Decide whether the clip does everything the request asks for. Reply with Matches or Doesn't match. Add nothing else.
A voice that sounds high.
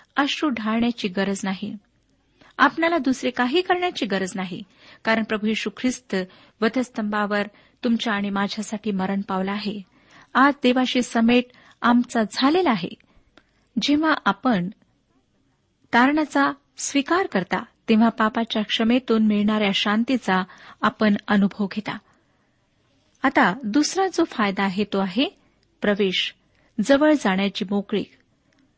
Matches